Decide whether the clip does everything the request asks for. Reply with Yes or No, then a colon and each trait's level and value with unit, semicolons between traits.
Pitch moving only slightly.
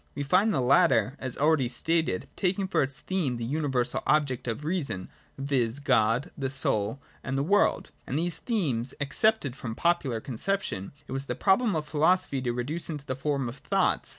No: average, 5.0 semitones